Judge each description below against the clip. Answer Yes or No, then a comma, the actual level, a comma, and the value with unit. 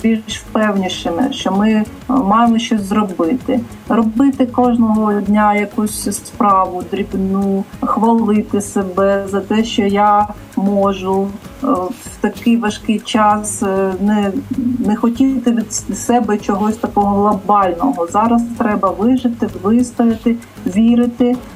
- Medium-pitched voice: No, high, 215 Hz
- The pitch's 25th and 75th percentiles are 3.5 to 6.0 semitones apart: No, average, 2.8 semitones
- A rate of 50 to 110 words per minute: Yes, slow, 105 wpm